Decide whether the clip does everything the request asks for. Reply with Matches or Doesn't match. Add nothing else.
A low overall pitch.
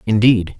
Matches